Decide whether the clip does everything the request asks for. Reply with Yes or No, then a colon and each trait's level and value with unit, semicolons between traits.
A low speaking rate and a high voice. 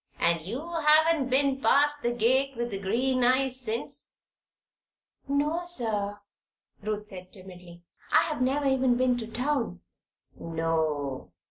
Yes: slow, 130 wpm; high, 245 Hz